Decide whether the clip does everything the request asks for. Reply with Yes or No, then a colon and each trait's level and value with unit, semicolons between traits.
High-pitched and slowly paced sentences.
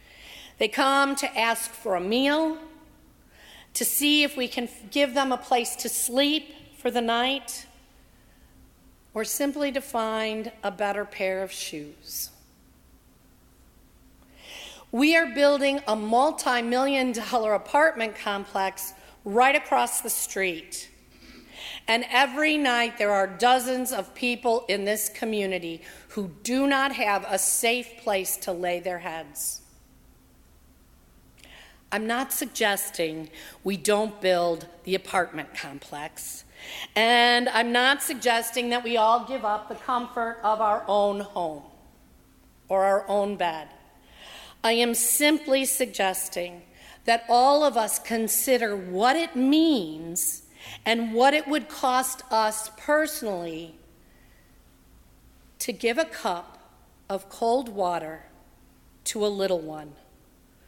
Yes: high, 225 Hz; slow, 120 wpm